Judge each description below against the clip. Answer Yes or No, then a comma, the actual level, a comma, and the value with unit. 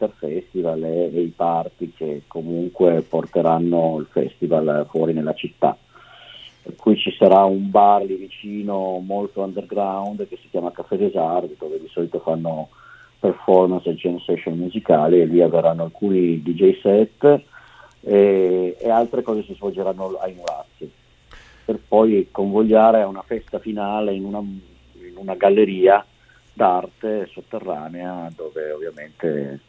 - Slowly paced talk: No, average, 135 wpm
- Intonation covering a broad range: No, average, 3.6 semitones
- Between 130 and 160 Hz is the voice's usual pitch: No, very low, 95 Hz